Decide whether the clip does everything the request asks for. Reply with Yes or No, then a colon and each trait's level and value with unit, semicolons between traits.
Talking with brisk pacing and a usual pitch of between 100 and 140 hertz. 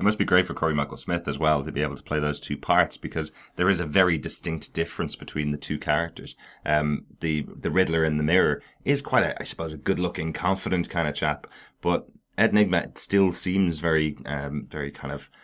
No: fast, 220 wpm; very low, 80 Hz